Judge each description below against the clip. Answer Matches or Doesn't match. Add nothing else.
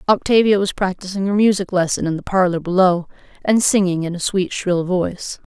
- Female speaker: Matches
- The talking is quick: Doesn't match